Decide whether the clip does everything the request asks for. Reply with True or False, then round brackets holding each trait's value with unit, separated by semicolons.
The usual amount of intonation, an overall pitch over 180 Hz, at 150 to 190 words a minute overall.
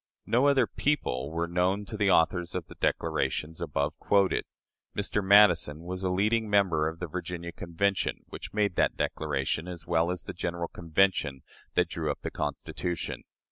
False (3.4 semitones; 90 Hz; 175 wpm)